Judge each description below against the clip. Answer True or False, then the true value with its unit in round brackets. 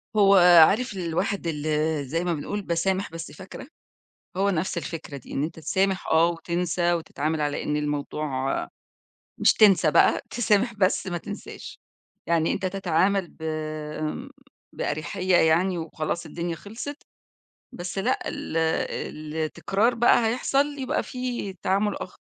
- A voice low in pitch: False (180 Hz)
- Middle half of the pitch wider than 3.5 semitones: True (3.9 semitones)